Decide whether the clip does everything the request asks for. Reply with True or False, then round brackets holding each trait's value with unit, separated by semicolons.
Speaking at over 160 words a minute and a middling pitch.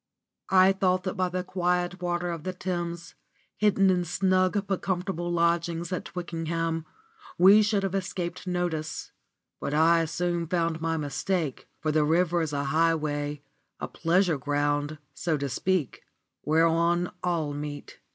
False (145 wpm; 170 Hz)